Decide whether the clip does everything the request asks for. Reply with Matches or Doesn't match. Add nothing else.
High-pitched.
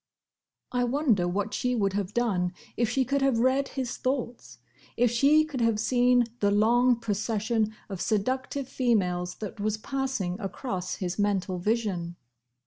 Matches